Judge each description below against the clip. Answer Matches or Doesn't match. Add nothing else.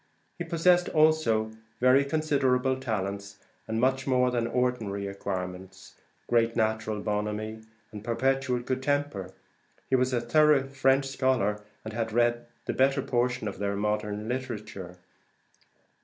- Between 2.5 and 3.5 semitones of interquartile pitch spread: Doesn't match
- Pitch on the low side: Matches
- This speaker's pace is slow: Matches